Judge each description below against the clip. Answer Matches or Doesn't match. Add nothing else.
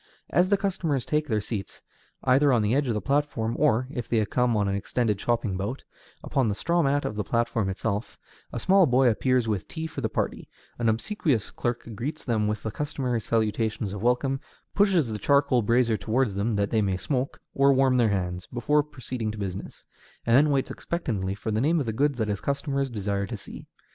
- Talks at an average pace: Doesn't match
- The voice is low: Matches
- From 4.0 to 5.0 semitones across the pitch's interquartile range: Matches